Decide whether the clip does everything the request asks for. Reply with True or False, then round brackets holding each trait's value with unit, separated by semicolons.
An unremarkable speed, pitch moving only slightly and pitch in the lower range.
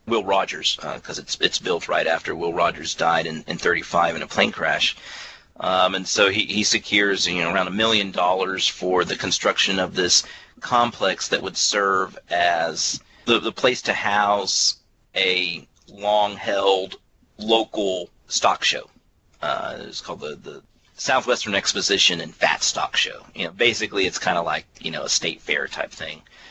True (175 wpm; 2.2 semitones; 95 Hz)